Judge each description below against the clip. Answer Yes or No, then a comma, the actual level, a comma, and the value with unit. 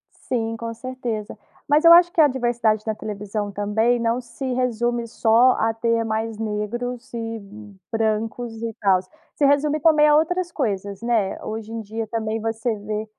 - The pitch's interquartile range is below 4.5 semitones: Yes, narrow, 2.5 semitones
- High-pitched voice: Yes, high, 225 Hz